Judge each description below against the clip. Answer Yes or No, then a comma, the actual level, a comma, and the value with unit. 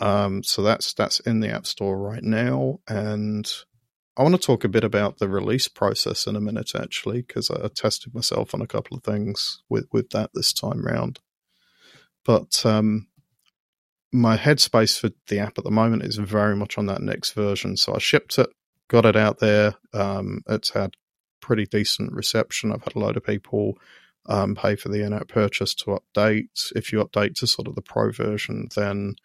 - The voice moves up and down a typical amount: No, narrow, 2.0 semitones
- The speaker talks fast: No, average, 195 wpm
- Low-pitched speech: Yes, low, 105 Hz